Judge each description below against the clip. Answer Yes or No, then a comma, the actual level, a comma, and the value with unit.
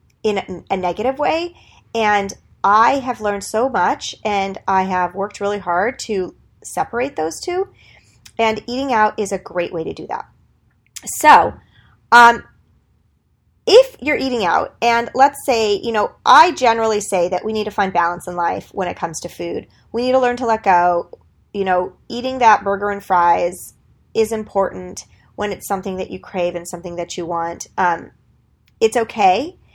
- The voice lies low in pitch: No, high, 205 Hz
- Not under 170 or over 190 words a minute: Yes, average, 175 wpm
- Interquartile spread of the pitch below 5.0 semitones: Yes, average, 4.6 semitones